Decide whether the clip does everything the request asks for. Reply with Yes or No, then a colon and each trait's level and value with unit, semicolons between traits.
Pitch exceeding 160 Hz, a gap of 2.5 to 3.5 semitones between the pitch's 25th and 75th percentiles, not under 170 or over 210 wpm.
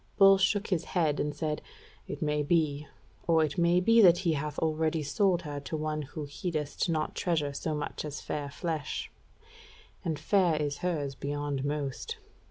No: medium, 155 Hz; average, 2.9 semitones; average, 175 wpm